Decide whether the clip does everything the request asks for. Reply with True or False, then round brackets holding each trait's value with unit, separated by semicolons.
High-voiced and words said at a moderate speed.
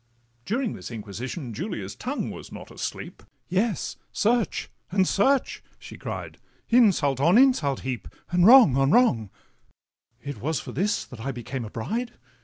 False (175 Hz; 145 wpm)